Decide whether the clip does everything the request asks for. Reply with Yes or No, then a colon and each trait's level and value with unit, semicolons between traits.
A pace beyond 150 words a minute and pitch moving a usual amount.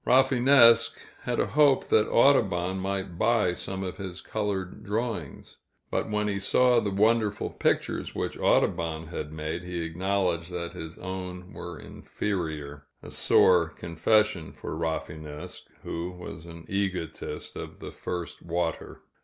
No: slow, 135 wpm; average, 4.0 semitones